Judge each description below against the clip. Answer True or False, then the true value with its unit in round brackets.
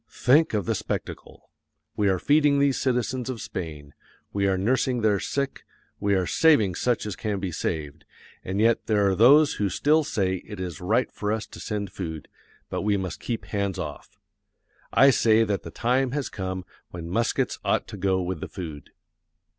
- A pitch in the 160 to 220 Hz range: False (105 Hz)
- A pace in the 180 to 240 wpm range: True (185 wpm)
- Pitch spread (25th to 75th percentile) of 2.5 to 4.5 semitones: False (4.9 semitones)